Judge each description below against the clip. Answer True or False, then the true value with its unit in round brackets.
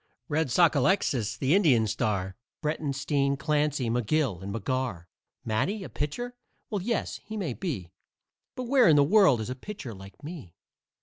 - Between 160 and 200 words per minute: False (150 wpm)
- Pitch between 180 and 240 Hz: False (140 Hz)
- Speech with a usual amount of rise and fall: False (7.2 semitones)